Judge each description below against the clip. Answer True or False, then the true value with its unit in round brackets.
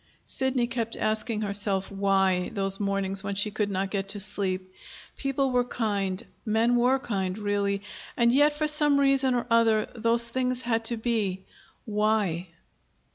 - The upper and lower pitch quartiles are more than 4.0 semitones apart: False (3.5 semitones)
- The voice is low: False (215 Hz)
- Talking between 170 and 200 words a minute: False (155 wpm)